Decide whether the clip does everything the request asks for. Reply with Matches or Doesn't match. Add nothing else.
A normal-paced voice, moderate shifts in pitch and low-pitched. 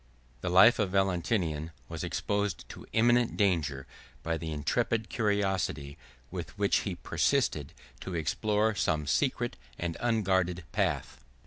Doesn't match